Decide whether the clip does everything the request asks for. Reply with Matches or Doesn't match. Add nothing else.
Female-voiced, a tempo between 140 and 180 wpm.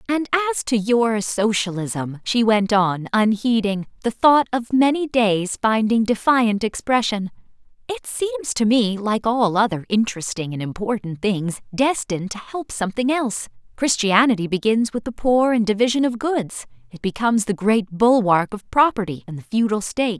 Matches